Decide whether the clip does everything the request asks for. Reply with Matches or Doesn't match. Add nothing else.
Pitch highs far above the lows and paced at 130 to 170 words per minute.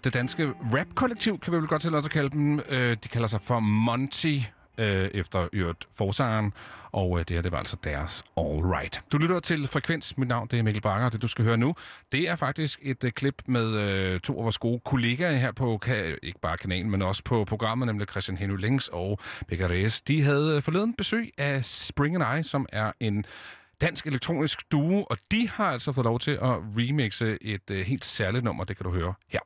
Doesn't match